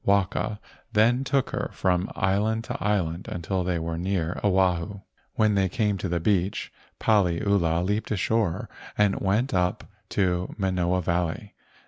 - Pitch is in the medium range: No, very low, 95 Hz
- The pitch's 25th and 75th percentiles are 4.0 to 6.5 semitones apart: No, average, 2.9 semitones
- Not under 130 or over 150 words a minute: Yes, average, 140 wpm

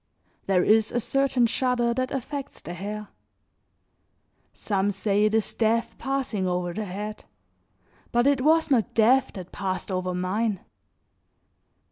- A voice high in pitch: Yes, high, 215 Hz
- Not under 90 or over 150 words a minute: Yes, slow, 135 wpm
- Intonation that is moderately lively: Yes, average, 4.5 semitones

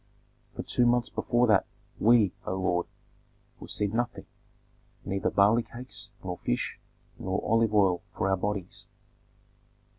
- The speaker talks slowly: Yes, slow, 125 wpm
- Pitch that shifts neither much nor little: Yes, average, 3.7 semitones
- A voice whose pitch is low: Yes, low, 105 Hz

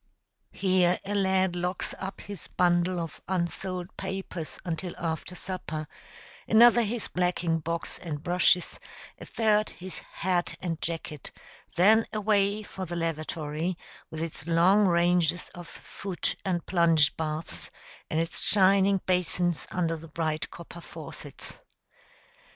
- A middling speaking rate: No, slow, 130 wpm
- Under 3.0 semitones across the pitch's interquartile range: Yes, narrow, 2.5 semitones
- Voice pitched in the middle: Yes, medium, 175 Hz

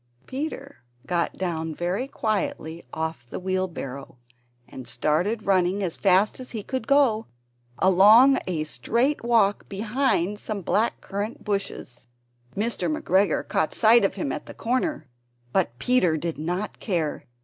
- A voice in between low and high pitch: No, high, 195 Hz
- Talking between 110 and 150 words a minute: Yes, average, 140 wpm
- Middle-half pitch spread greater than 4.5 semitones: Yes, wide, 5.4 semitones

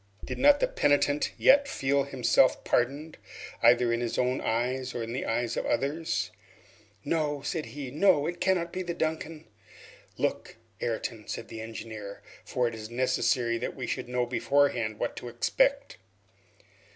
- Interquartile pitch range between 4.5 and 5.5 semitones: Yes, average, 4.9 semitones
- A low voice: Yes, low, 130 Hz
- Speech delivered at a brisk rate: No, average, 165 wpm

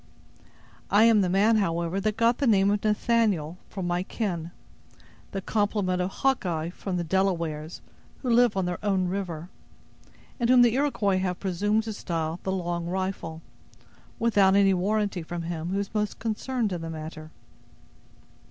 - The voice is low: No, high, 190 Hz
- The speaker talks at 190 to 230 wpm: No, average, 160 wpm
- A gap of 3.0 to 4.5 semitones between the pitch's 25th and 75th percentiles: Yes, average, 3.6 semitones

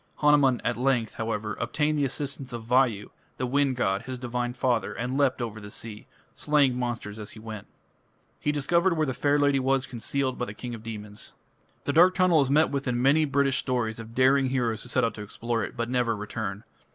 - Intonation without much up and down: No, average, 3.6 semitones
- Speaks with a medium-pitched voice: No, low, 125 Hz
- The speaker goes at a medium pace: No, fast, 210 wpm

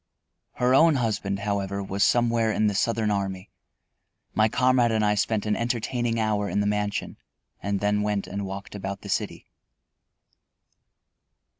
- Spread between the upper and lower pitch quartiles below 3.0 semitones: Yes, narrow, 2.4 semitones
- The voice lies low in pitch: Yes, low, 105 Hz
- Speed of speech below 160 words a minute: Yes, average, 150 wpm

